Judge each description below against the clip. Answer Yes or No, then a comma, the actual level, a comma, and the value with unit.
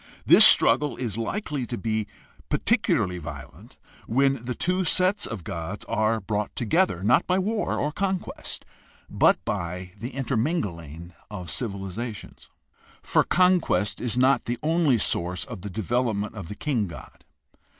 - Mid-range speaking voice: No, low, 115 Hz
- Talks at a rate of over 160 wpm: No, average, 145 wpm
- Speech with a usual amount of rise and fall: No, wide, 6.7 semitones